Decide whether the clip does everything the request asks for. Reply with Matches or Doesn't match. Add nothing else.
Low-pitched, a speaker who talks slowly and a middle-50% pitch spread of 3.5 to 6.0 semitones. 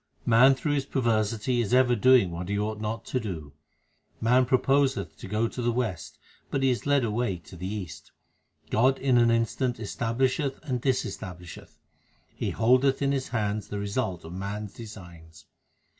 Doesn't match